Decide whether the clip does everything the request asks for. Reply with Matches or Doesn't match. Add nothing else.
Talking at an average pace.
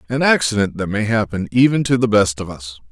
Doesn't match